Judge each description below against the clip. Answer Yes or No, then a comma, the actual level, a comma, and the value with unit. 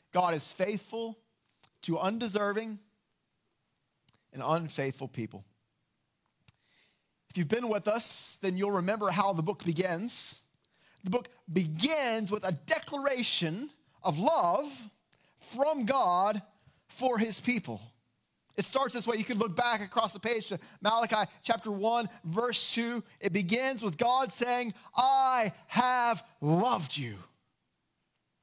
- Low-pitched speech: No, high, 210 Hz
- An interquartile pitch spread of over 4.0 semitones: Yes, average, 5.1 semitones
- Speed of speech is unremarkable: No, slow, 125 wpm